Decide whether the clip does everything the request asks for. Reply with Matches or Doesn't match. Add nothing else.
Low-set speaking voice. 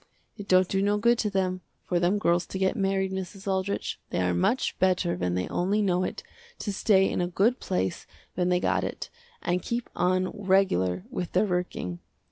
Doesn't match